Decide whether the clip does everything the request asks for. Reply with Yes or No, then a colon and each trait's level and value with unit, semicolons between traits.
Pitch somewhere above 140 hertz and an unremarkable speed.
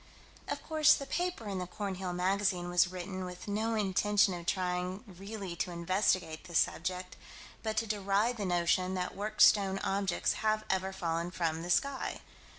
Yes: high, 190 Hz; average, 165 wpm